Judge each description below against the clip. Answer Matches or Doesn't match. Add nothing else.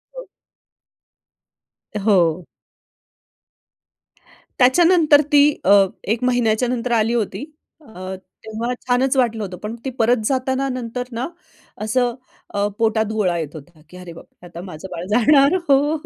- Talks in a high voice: Matches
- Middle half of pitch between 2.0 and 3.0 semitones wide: Doesn't match